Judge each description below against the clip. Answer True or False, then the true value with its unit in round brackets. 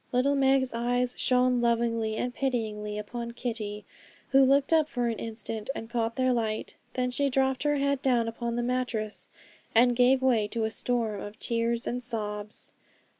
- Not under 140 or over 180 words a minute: True (175 wpm)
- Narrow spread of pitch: True (2.1 semitones)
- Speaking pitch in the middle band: False (240 Hz)